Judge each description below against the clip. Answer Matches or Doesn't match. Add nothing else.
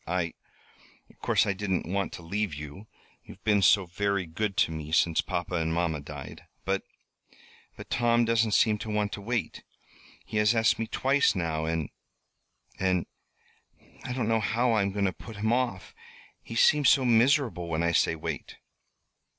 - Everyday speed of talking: Matches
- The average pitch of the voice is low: Matches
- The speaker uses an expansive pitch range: Doesn't match